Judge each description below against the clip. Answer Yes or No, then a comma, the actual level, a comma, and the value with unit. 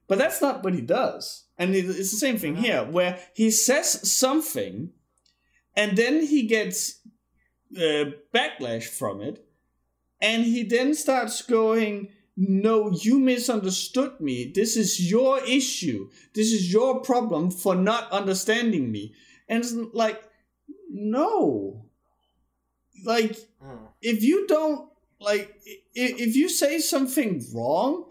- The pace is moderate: No, slow, 125 wpm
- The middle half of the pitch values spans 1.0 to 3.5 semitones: No, average, 5.2 semitones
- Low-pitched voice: No, high, 220 Hz